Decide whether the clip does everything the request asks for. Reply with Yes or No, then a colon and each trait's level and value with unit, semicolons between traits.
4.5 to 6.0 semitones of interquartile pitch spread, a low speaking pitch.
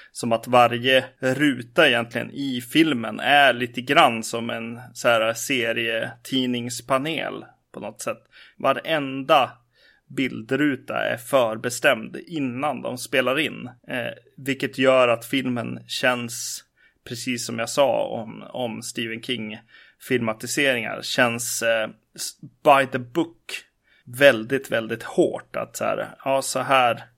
No: narrow, 2.4 semitones; low, 125 Hz